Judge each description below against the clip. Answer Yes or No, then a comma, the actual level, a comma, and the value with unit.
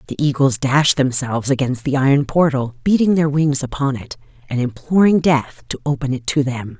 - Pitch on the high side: No, medium, 140 Hz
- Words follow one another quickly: No, average, 185 wpm